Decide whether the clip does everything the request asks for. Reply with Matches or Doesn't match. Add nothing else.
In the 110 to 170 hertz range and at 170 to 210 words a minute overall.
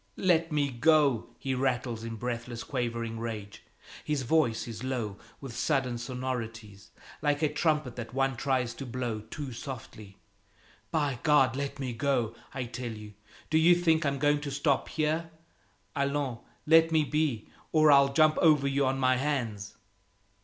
Doesn't match